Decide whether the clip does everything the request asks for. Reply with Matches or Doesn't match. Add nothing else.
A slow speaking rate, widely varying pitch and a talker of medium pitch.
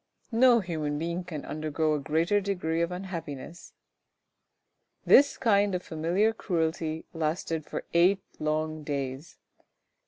Doesn't match